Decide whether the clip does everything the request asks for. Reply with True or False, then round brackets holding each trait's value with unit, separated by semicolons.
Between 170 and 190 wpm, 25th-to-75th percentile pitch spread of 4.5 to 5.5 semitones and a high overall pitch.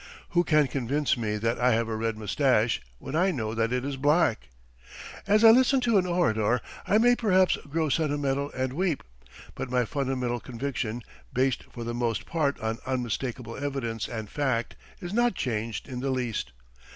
False (175 wpm; 4.8 semitones; 130 Hz)